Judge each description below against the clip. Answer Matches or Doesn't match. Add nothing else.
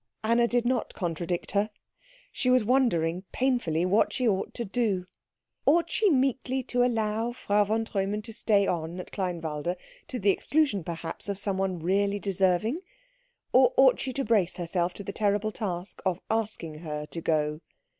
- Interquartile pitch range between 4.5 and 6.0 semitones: Matches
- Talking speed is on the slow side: Doesn't match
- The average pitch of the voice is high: Matches